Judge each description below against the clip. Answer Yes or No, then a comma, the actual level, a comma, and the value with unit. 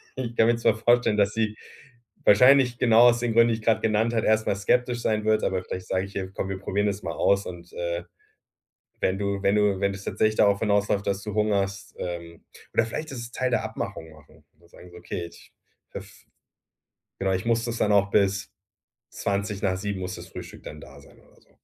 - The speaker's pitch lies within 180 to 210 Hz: No, low, 100 Hz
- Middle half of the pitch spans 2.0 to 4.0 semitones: Yes, average, 2.9 semitones